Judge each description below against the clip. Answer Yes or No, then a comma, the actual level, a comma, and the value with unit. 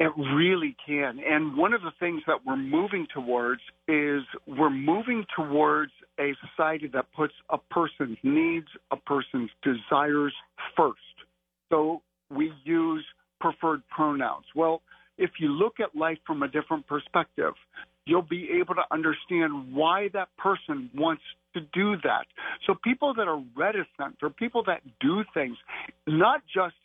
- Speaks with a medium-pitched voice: Yes, medium, 160 Hz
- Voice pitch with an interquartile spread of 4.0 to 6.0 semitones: Yes, average, 4.8 semitones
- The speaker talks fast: No, average, 150 wpm